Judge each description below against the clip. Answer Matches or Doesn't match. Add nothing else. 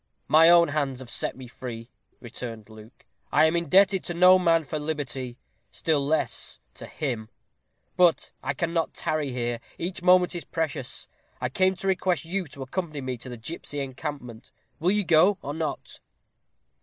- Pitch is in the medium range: Matches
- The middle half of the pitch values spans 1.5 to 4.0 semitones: Doesn't match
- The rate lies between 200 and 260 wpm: Doesn't match